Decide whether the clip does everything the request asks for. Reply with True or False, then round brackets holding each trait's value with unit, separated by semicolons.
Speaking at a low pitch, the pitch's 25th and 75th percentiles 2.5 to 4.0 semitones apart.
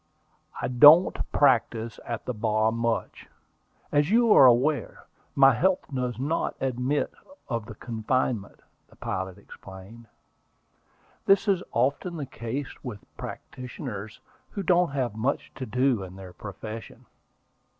False (125 Hz; 4.4 semitones)